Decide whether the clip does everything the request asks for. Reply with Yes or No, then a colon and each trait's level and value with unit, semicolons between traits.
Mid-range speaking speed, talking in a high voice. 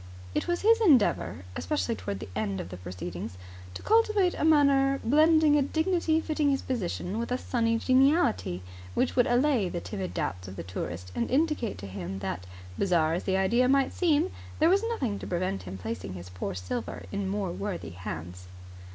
Yes: average, 185 wpm; high, 200 Hz